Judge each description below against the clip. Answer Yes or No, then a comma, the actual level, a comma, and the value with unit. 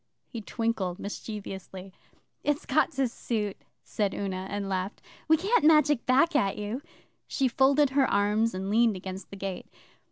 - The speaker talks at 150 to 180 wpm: Yes, average, 155 wpm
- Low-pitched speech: No, high, 215 Hz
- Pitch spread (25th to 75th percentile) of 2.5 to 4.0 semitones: No, wide, 5.5 semitones